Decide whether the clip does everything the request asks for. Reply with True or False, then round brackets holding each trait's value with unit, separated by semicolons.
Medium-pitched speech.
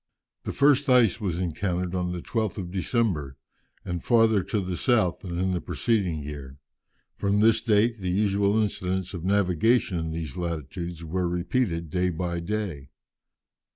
False (90 Hz)